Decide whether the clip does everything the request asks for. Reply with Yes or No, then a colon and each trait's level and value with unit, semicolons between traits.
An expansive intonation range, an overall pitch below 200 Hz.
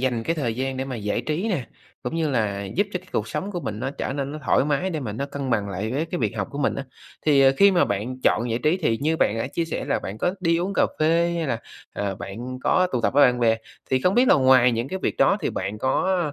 Yes: wide, 6.4 semitones; low, 135 Hz